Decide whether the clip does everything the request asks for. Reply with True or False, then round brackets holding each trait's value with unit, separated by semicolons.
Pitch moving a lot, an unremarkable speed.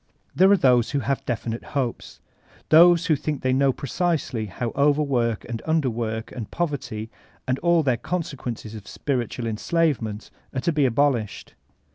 False (4.7 semitones; 155 wpm)